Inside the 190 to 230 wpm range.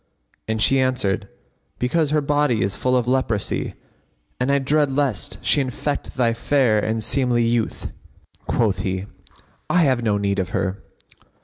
No: average, 150 wpm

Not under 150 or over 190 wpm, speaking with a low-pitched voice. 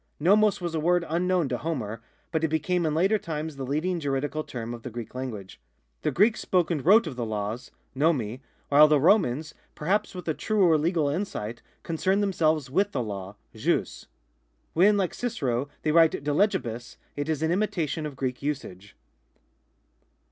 No: average, 175 wpm; medium, 155 Hz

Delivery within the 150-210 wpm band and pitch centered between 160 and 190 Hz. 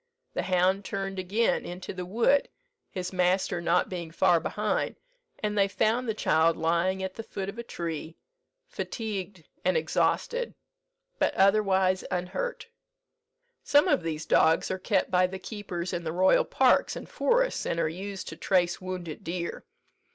Yes: average, 160 wpm; medium, 185 Hz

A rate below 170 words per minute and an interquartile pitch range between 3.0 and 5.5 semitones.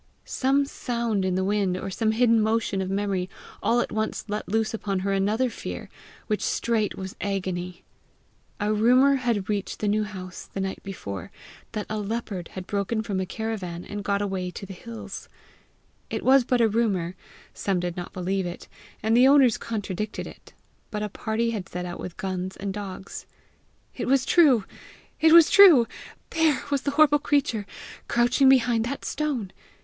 No: average, 175 wpm; average, 3.8 semitones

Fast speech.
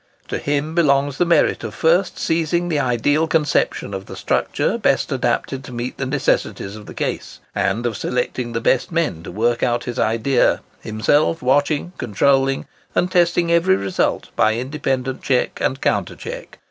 No: average, 170 wpm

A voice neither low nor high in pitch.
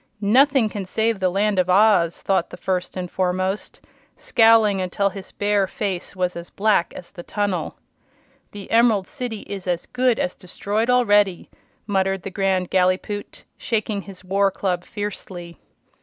No: high, 195 Hz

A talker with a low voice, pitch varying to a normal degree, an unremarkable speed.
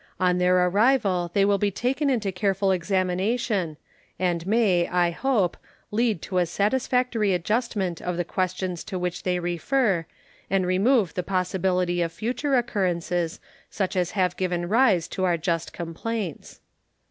No: medium, 185 Hz; average, 3.2 semitones; average, 145 wpm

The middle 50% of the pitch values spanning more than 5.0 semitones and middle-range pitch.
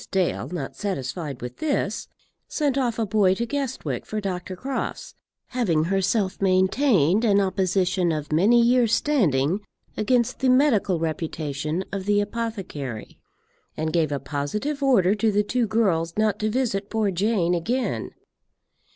No: wide, 5.4 semitones; high, 195 Hz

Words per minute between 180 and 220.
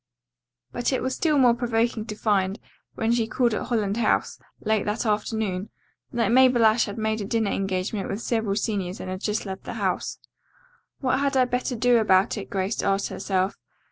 Yes: average, 190 wpm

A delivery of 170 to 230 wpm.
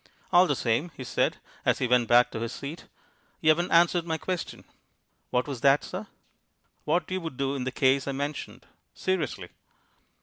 Yes: average, 180 wpm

